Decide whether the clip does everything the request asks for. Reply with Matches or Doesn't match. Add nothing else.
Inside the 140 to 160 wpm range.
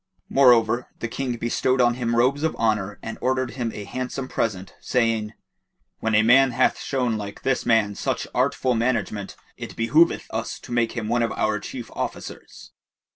Doesn't match